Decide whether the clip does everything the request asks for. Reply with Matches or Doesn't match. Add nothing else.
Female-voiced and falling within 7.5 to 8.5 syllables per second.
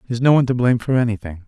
Doesn't match